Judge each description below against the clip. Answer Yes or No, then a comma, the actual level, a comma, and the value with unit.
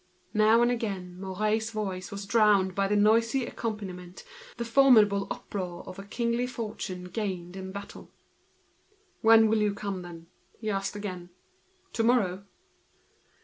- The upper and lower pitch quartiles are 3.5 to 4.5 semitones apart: No, average, 3.0 semitones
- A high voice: Yes, high, 205 Hz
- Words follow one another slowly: No, average, 145 wpm